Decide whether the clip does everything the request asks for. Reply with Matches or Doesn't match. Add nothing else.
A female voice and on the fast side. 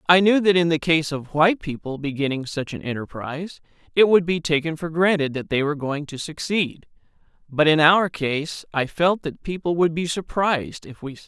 Doesn't match